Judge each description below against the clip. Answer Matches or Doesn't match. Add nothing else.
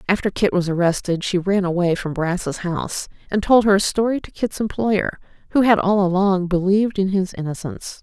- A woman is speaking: Matches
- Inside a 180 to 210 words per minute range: Matches